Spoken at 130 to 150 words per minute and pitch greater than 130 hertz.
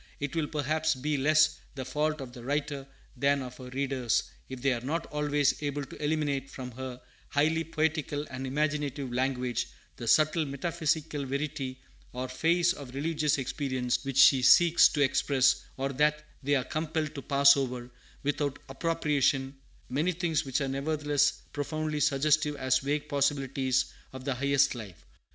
No: average, 160 wpm; medium, 140 Hz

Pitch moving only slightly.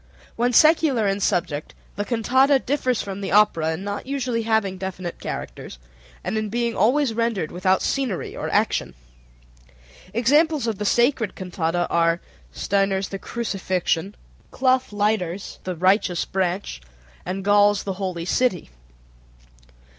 No: average, 4.3 semitones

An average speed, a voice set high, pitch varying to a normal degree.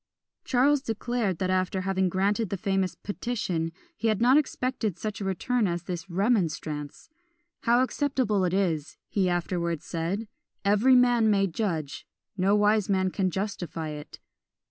Yes: average, 145 wpm; high, 195 Hz; average, 4.2 semitones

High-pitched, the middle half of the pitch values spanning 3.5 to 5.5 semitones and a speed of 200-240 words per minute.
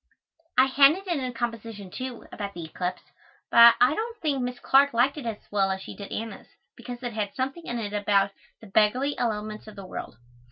Yes: high, 235 Hz; average, 4.3 semitones; fast, 205 wpm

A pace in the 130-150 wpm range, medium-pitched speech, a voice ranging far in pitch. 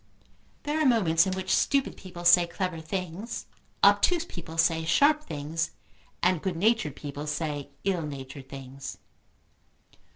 No: slow, 135 wpm; medium, 170 Hz; average, 4.3 semitones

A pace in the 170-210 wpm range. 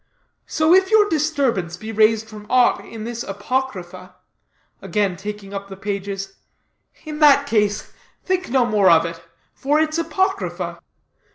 No: average, 145 wpm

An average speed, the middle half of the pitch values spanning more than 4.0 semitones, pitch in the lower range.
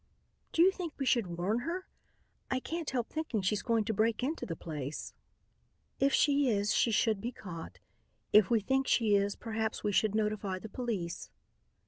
No: average, 180 wpm; average, 4.6 semitones; high, 220 Hz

